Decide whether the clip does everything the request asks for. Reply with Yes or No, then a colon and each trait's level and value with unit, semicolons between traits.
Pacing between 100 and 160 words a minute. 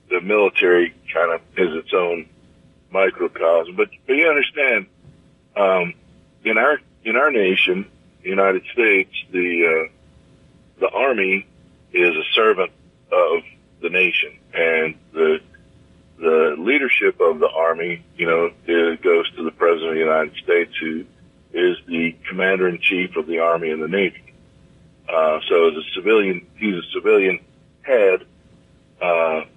Yes: average, 145 wpm